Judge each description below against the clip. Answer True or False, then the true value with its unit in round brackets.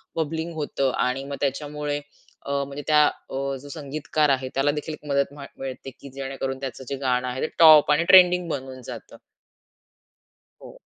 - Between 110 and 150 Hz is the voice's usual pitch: True (140 Hz)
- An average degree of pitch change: False (2.1 semitones)